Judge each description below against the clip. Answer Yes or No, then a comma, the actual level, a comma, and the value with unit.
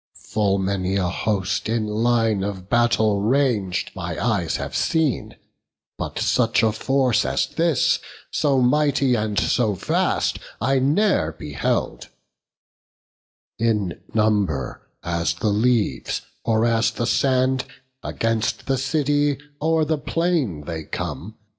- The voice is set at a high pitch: No, low, 115 Hz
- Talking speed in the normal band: No, slow, 120 wpm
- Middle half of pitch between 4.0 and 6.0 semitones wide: Yes, average, 4.9 semitones